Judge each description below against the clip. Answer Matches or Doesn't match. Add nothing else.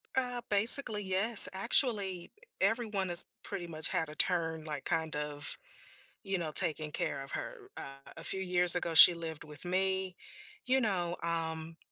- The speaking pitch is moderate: Matches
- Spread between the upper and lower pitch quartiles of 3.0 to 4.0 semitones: Matches